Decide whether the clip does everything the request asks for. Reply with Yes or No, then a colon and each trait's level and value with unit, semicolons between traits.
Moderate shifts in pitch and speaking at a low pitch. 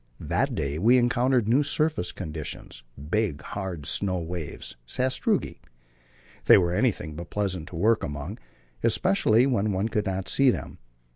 No: wide, 6.0 semitones; very low, 95 Hz